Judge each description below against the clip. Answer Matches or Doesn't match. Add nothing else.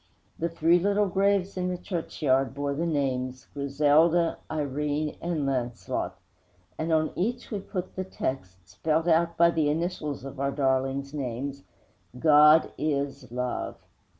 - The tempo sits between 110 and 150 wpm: Matches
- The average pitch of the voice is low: Doesn't match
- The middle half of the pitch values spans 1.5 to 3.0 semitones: Doesn't match